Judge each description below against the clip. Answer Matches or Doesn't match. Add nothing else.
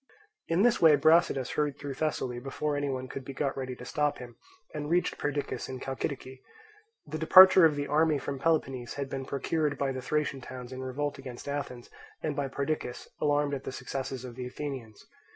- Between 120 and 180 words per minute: Doesn't match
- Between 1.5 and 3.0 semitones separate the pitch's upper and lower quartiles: Matches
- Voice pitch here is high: Doesn't match